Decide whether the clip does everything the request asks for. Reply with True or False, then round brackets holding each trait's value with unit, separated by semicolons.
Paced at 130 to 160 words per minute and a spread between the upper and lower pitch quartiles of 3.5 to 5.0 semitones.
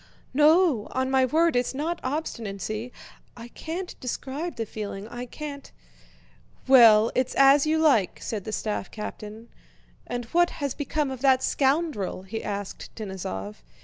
False (145 wpm; 5.4 semitones)